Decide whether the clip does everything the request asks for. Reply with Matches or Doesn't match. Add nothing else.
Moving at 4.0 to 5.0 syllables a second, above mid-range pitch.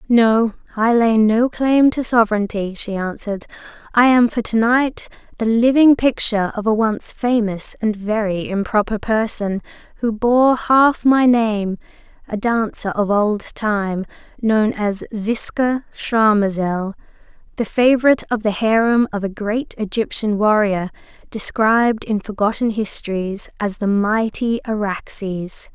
Matches